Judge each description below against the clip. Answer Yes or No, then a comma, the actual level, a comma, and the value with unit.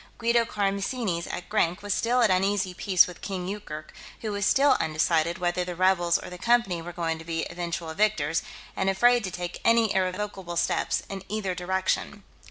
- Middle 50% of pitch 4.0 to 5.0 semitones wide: No, average, 3.2 semitones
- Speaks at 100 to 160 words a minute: No, average, 185 wpm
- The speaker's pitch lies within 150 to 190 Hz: Yes, medium, 185 Hz